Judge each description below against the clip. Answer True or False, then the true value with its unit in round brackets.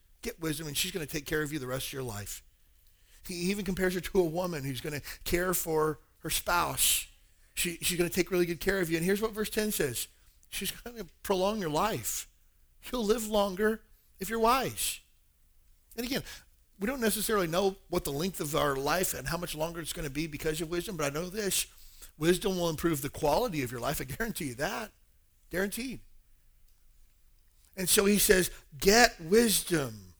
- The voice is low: False (170 Hz)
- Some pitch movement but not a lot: False (7.1 semitones)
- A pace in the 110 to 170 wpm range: False (205 wpm)